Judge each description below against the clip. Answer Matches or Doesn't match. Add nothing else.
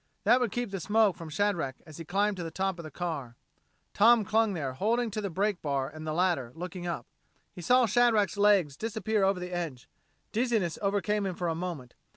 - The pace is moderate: Doesn't match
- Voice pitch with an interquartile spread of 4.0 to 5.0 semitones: Matches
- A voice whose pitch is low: Doesn't match